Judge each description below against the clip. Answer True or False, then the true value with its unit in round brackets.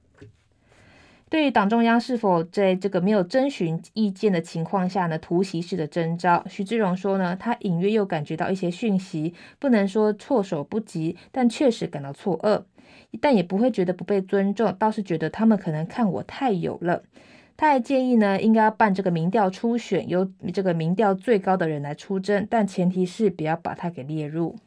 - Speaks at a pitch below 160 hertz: False (195 Hz)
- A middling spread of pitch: True (4.1 semitones)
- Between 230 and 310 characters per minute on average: True (285 characters per minute)